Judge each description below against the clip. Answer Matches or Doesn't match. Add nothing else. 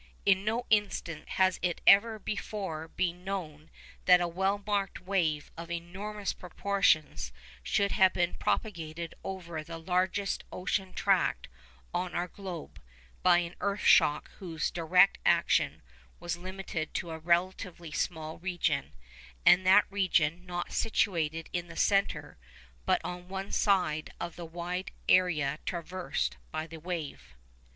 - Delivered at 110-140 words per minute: Matches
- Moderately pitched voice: Matches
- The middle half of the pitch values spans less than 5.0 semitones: Matches